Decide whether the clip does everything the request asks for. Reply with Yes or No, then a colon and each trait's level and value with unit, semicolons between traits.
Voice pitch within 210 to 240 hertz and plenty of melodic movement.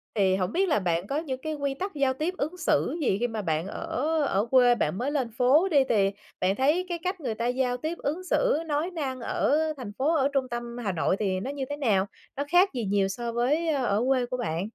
No: very high, 260 Hz; wide, 5.9 semitones